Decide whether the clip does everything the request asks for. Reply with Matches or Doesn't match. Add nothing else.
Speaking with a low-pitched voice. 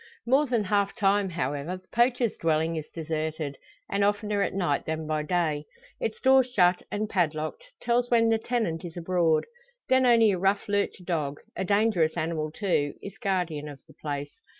Doesn't match